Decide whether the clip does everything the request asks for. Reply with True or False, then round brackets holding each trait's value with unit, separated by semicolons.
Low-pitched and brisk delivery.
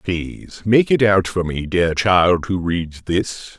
False (95 Hz; 185 wpm)